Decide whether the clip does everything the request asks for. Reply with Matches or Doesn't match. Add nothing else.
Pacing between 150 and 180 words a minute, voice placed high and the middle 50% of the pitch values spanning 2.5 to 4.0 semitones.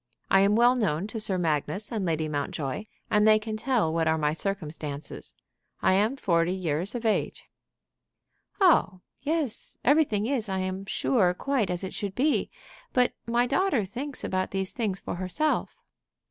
Doesn't match